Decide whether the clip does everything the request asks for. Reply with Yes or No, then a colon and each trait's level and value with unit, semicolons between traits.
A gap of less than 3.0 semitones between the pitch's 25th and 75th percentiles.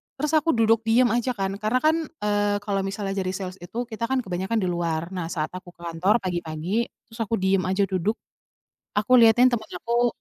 No: average, 3.8 semitones